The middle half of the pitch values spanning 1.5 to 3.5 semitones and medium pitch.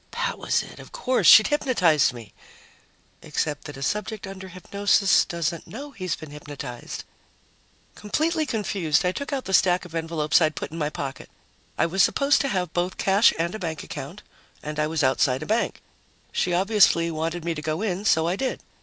No: average, 5.0 semitones; medium, 175 Hz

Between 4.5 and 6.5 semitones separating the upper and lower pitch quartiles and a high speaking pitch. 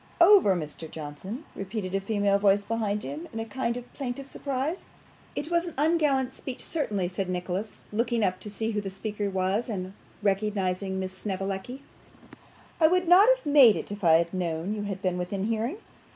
Yes: wide, 5.5 semitones; high, 210 Hz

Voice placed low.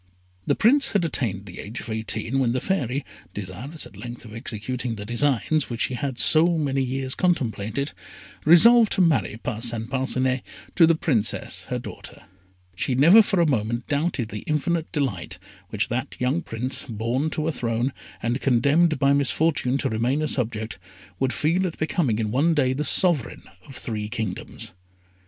Yes: low, 130 Hz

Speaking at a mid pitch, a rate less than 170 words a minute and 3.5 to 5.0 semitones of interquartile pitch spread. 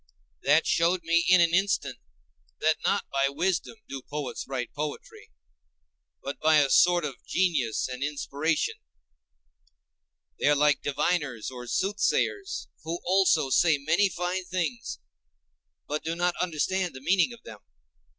Yes: medium, 160 Hz; average, 140 wpm; average, 4.4 semitones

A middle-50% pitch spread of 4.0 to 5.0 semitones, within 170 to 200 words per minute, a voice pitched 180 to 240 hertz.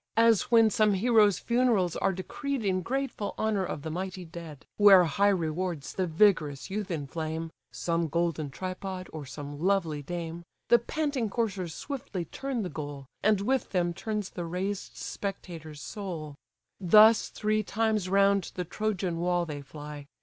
No: average, 4.4 semitones; average, 155 wpm; medium, 185 Hz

